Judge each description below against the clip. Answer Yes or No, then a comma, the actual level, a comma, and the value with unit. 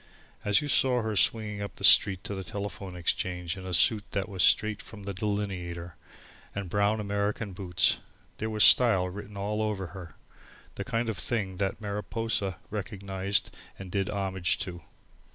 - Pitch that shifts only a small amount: Yes, narrow, 2.1 semitones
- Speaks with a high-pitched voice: No, low, 100 Hz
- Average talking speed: Yes, average, 170 wpm